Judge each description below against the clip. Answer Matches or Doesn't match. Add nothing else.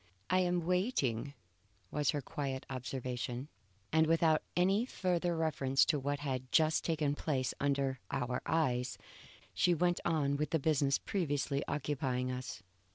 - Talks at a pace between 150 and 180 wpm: Doesn't match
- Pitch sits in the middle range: Matches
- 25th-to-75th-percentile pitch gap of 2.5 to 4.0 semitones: Matches